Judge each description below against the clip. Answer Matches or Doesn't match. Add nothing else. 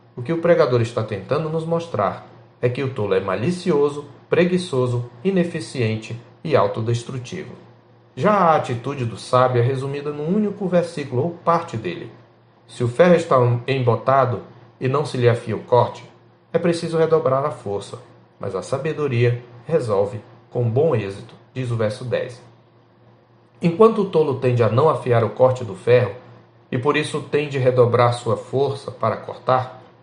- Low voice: Matches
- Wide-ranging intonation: Doesn't match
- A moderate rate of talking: Matches